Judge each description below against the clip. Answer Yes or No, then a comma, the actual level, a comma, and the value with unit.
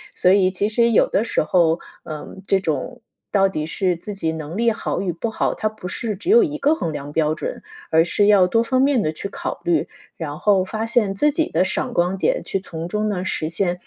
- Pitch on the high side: Yes, high, 195 Hz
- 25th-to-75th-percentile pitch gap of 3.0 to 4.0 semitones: No, average, 4.6 semitones